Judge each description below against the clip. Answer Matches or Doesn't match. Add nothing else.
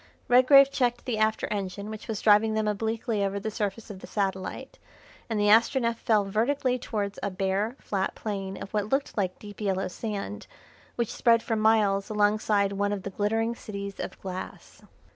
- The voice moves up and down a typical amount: Doesn't match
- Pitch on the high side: Matches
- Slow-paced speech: Doesn't match